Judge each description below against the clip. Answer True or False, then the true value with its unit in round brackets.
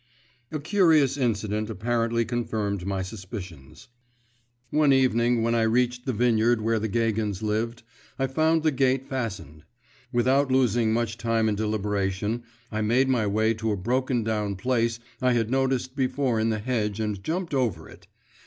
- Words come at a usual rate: True (160 wpm)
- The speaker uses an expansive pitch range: False (3.2 semitones)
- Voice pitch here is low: True (115 Hz)